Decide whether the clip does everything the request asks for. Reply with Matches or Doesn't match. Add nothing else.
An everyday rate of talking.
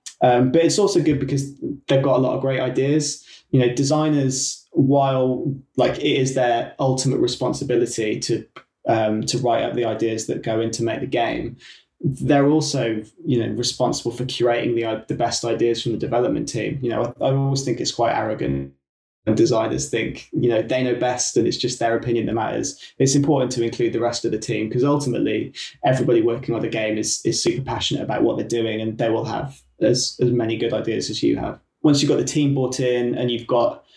Doesn't match